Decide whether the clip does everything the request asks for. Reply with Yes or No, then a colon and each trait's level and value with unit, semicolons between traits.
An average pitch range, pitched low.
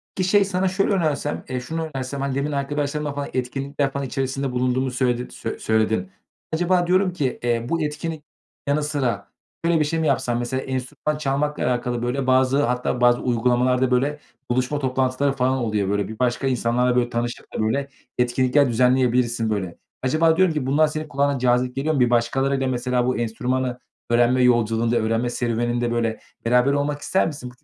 Yes: average, 3.0 semitones; low, 130 Hz